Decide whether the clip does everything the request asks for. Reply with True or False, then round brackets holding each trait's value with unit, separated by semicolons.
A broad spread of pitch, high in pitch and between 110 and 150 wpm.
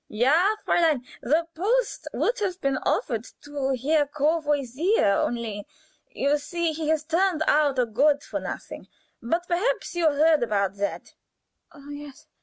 False (4.6 semitones; 295 Hz; 135 wpm)